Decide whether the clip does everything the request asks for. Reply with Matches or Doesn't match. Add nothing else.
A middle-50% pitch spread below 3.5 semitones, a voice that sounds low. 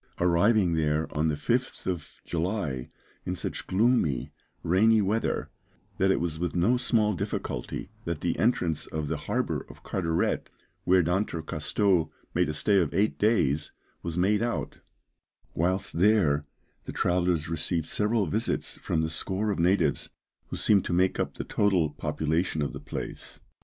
Doesn't match